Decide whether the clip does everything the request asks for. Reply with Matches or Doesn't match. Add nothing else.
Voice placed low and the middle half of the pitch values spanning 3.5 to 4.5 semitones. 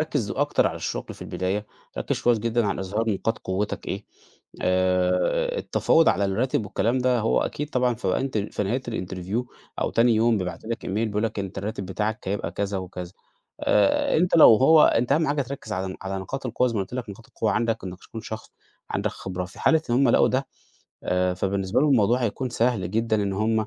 Matches